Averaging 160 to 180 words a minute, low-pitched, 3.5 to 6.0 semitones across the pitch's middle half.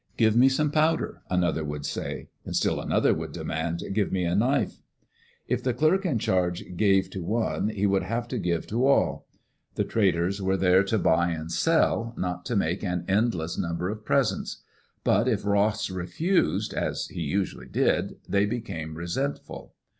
Yes: average, 170 wpm; low, 100 Hz; average, 4.8 semitones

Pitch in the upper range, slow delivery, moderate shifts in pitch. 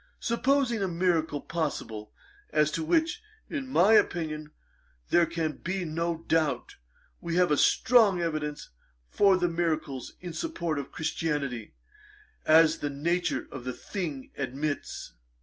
No: medium, 165 Hz; slow, 130 wpm; average, 3.3 semitones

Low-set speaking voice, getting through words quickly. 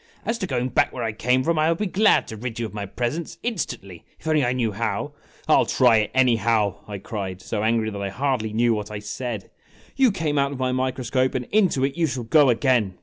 Yes: low, 125 Hz; fast, 260 wpm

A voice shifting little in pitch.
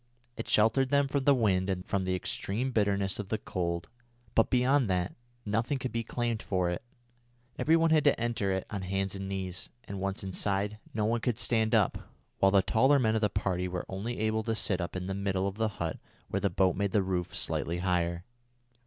No: average, 3.5 semitones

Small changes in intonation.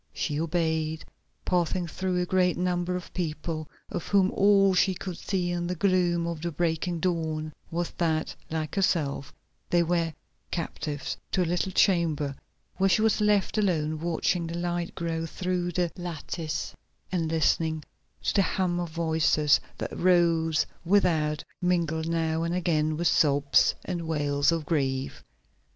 Yes: narrow, 2.2 semitones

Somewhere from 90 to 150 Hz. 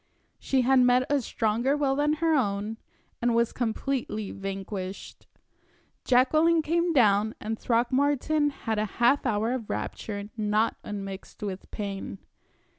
No: high, 235 Hz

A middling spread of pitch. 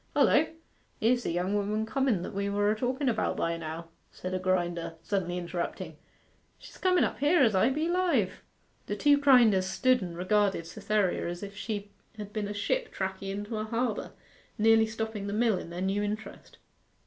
Yes: average, 3.7 semitones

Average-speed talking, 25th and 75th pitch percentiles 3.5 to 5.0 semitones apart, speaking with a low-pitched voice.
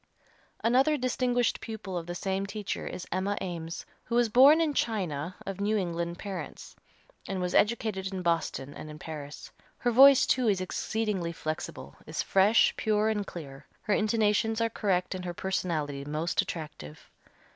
No: average, 160 wpm; average, 4.6 semitones; high, 190 Hz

